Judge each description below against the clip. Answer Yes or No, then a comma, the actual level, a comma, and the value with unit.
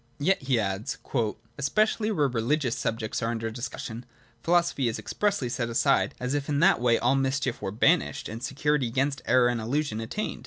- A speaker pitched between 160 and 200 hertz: No, low, 130 Hz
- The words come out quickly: Yes, fast, 210 wpm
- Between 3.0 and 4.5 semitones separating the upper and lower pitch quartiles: Yes, average, 4.0 semitones